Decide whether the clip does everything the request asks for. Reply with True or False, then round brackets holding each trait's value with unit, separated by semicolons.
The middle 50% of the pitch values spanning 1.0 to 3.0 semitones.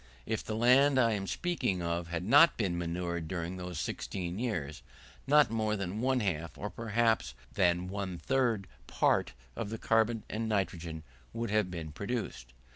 False (4.8 semitones)